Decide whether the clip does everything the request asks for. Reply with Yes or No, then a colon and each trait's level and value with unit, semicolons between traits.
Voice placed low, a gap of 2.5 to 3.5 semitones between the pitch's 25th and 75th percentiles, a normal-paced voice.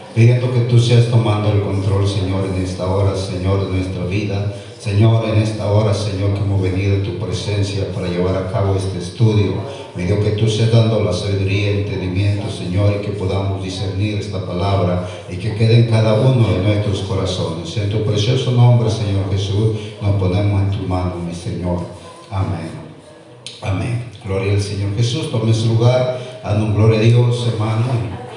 Yes: low, 100 Hz; average, 2.8 semitones; average, 180 wpm